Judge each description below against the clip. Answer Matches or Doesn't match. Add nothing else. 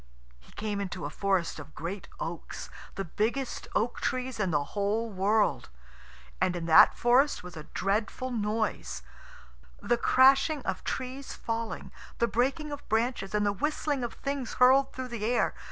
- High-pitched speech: Matches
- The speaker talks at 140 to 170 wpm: Matches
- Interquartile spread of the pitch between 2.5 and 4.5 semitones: Doesn't match